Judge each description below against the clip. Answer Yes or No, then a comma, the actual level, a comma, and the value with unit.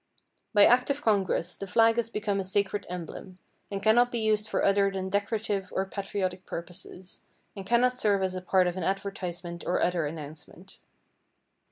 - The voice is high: Yes, high, 195 Hz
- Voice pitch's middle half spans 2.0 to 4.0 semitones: Yes, average, 2.7 semitones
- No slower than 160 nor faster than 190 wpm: Yes, average, 175 wpm